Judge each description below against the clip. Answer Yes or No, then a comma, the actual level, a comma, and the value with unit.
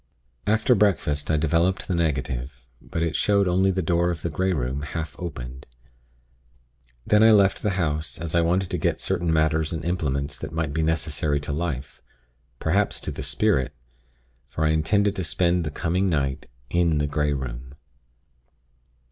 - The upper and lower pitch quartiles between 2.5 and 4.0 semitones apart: Yes, average, 3.6 semitones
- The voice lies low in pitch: Yes, very low, 80 Hz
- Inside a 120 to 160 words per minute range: No, average, 170 wpm